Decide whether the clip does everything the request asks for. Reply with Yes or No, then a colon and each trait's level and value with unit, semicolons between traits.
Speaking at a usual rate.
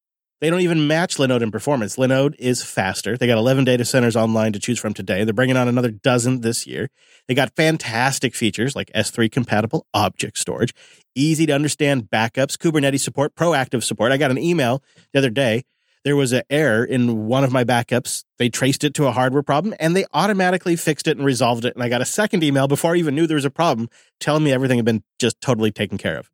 No: fast, 225 wpm